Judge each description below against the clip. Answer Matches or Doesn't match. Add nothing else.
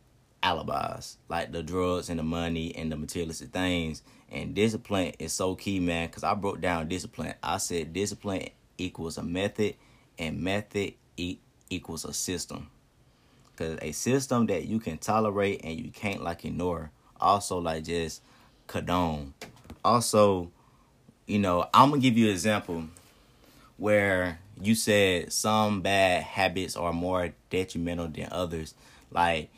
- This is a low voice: Matches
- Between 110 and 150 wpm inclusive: Matches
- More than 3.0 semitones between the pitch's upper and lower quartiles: Matches